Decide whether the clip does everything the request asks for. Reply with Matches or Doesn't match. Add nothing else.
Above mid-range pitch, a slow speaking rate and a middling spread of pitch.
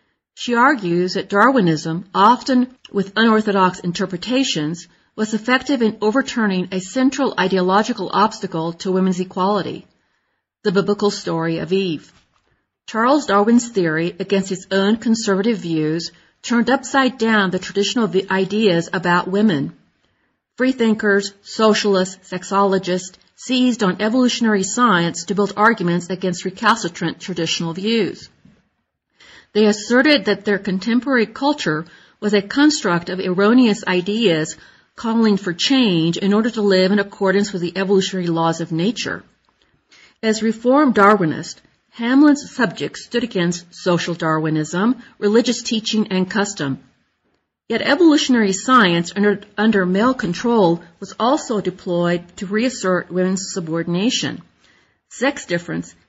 Matches